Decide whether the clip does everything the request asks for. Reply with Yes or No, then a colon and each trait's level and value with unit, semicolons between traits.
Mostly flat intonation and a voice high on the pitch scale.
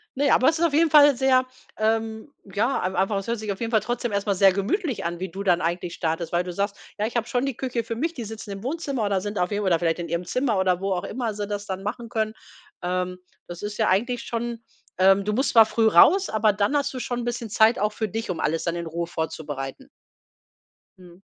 No: average, 4.6 semitones; high, 210 Hz